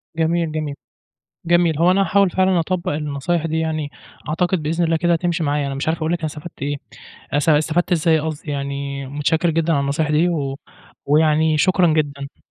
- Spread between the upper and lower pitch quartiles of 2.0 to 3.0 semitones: Yes, narrow, 2.6 semitones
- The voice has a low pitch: No, medium, 160 Hz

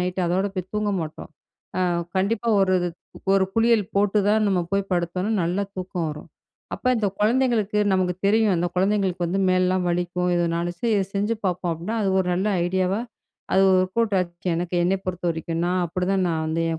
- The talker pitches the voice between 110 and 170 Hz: No, medium, 185 Hz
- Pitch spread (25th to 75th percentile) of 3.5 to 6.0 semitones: No, narrow, 2.4 semitones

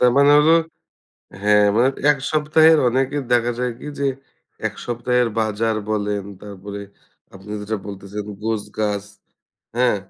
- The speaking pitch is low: Yes, low, 115 Hz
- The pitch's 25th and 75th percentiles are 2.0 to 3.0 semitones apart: No, average, 3.7 semitones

